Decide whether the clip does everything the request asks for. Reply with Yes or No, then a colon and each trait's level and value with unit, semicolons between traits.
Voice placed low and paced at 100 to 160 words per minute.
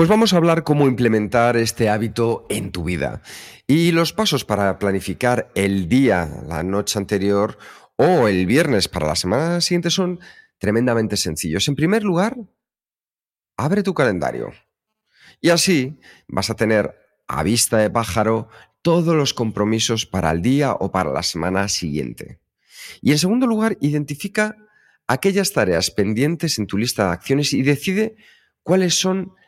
Yes: low, 120 Hz; average, 150 wpm